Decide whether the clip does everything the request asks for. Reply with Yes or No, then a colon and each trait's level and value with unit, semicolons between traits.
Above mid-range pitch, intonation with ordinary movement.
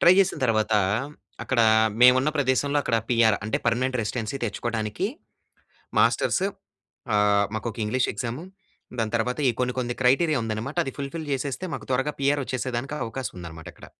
No: low, 125 Hz; average, 3.5 semitones